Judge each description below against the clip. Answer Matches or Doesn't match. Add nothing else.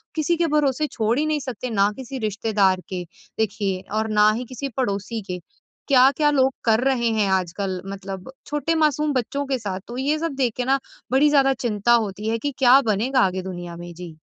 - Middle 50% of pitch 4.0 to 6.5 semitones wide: Matches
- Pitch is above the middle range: Matches